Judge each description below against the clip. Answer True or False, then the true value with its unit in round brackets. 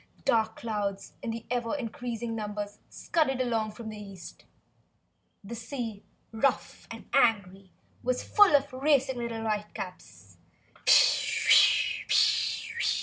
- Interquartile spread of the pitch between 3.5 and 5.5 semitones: False (3.1 semitones)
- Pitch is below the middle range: False (225 Hz)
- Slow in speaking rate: True (100 wpm)